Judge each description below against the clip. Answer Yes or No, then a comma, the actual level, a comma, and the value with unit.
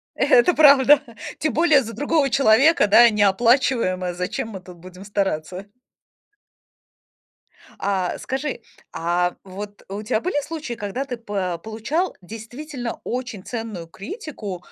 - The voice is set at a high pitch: Yes, high, 220 Hz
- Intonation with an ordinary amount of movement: No, wide, 6.4 semitones